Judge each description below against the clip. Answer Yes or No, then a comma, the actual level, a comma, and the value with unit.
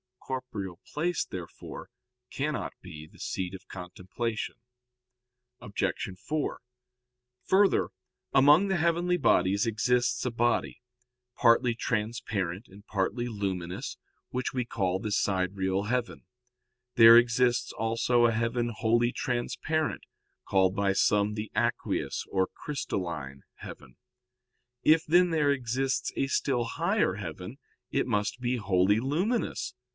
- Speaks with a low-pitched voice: Yes, low, 115 Hz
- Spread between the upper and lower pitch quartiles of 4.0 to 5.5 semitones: Yes, average, 5.1 semitones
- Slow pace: Yes, slow, 115 wpm